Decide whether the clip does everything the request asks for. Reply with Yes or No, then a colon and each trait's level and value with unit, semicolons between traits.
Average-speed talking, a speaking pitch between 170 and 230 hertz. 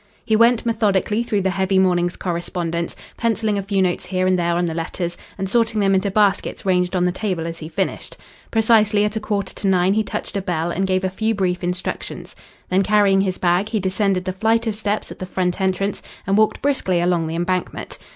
No: fast, 220 wpm; high, 190 Hz